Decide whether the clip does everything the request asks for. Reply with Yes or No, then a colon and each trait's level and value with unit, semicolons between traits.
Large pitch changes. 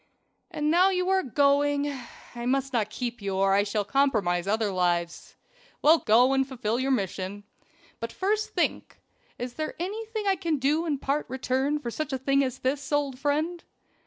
No: average, 4.8 semitones